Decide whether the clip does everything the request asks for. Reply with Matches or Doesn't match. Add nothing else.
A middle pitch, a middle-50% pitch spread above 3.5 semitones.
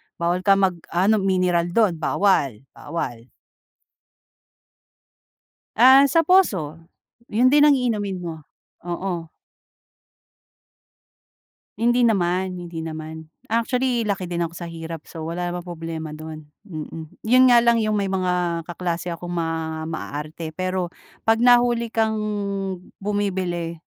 Matches